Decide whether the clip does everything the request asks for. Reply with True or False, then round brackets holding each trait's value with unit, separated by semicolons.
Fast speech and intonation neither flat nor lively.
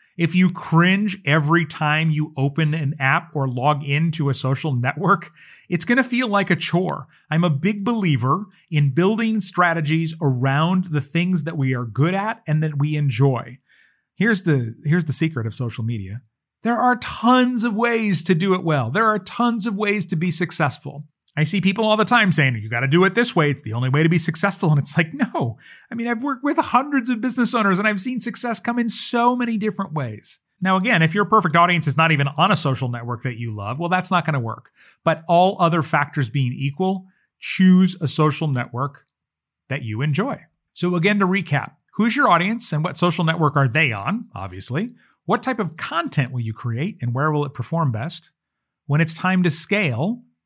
False (210 wpm; 5.8 semitones)